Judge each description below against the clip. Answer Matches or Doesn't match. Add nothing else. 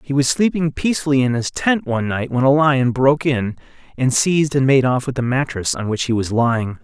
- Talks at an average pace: Doesn't match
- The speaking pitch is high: Doesn't match